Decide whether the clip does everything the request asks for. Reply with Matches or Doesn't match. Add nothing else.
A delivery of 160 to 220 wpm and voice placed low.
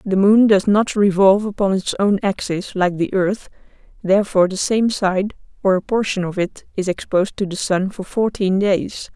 Doesn't match